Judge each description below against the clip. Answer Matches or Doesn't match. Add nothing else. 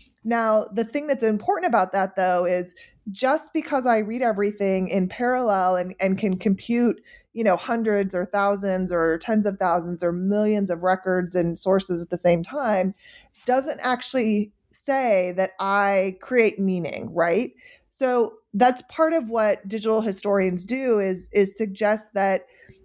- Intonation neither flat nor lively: Matches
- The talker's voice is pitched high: Matches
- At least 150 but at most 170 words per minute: Matches